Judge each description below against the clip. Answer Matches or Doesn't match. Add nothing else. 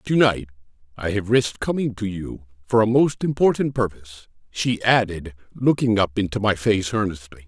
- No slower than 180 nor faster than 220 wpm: Doesn't match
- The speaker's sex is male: Matches